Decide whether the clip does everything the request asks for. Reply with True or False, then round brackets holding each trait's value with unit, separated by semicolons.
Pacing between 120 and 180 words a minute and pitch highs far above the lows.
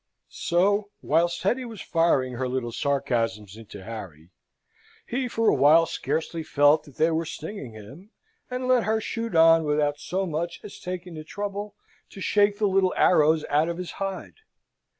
True (170 wpm; 5.9 semitones)